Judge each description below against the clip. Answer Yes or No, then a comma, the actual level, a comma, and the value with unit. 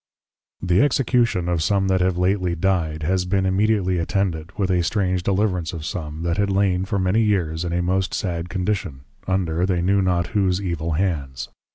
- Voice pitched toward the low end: Yes, very low, 90 Hz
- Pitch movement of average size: No, narrow, 2.3 semitones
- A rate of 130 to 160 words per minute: No, average, 190 wpm